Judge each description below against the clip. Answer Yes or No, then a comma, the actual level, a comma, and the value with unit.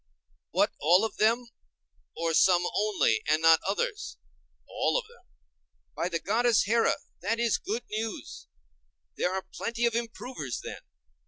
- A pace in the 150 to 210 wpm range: No, slow, 135 wpm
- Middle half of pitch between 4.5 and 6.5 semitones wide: Yes, average, 5.1 semitones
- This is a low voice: No, high, 215 Hz